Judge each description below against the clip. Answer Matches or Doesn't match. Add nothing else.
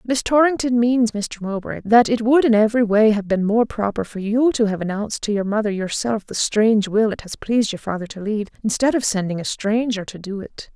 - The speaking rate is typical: Doesn't match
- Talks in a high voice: Matches